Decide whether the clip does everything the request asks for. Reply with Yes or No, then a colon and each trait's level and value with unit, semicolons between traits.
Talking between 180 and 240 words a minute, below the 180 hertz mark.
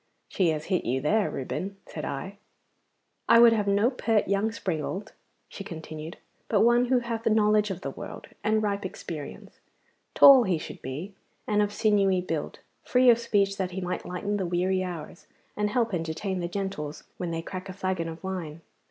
No: average, 185 wpm; high, 195 Hz